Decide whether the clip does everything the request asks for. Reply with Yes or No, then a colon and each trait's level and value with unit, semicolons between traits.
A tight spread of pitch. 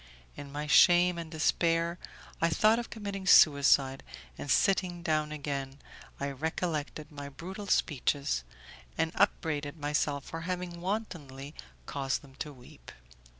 No: average, 3.7 semitones